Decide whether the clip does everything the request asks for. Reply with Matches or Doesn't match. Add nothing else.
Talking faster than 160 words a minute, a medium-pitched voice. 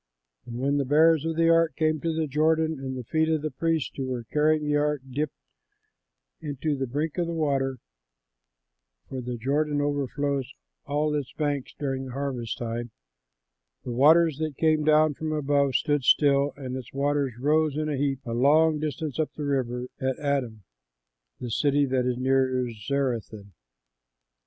Matches